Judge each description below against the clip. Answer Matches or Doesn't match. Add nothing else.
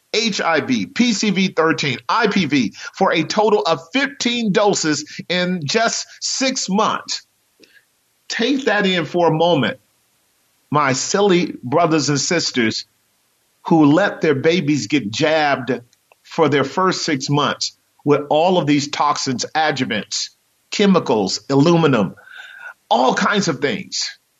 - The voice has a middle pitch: Matches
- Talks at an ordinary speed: Doesn't match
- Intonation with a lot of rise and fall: Matches